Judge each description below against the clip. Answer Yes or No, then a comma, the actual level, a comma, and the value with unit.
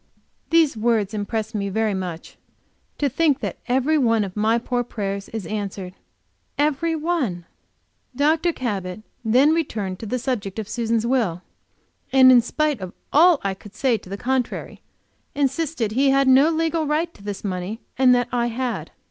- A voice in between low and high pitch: No, high, 240 Hz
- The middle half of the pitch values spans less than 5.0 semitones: No, wide, 5.4 semitones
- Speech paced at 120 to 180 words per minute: Yes, average, 170 wpm